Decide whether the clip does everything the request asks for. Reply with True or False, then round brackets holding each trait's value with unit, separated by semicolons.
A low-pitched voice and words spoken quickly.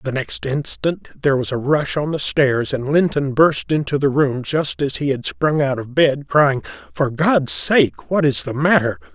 False (145 Hz; 210 wpm)